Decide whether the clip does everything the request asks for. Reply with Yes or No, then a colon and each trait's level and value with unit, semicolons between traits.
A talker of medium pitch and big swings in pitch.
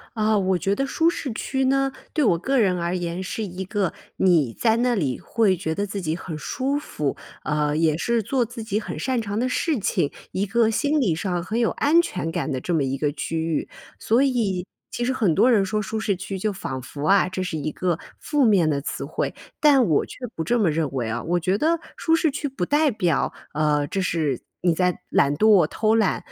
No: high, 195 Hz; wide, 6.3 semitones